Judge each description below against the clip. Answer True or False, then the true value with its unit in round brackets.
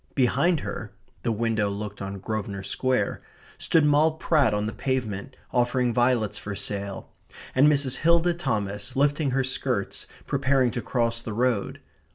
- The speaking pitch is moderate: False (125 Hz)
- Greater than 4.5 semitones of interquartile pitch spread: True (4.9 semitones)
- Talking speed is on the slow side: False (150 wpm)